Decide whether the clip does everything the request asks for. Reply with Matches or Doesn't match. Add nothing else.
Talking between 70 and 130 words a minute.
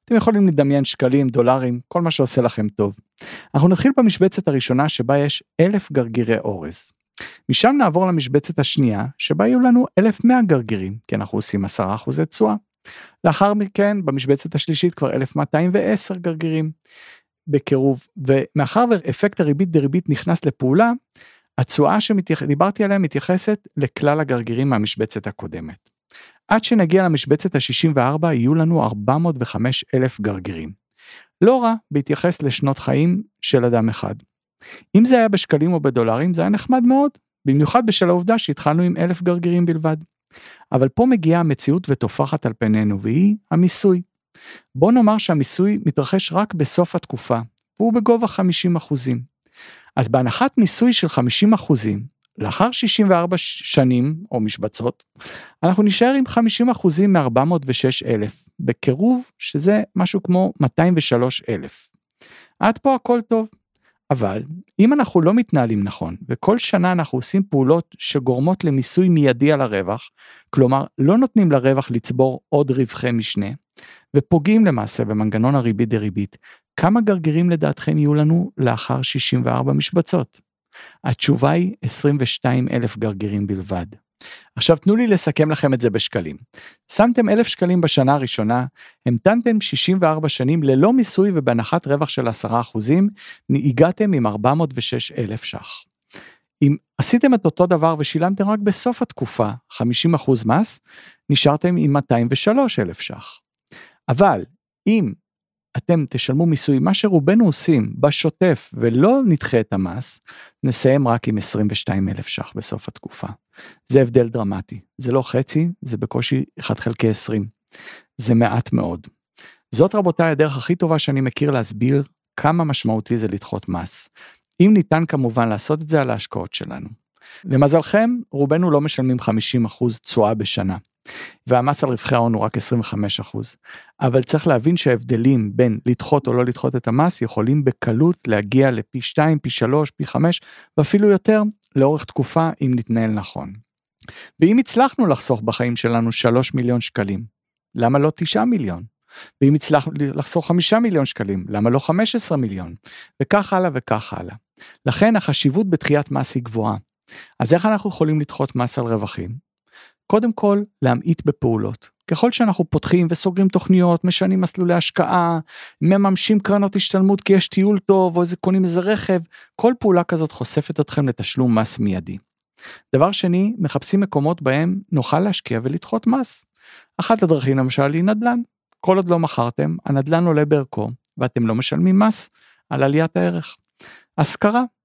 Doesn't match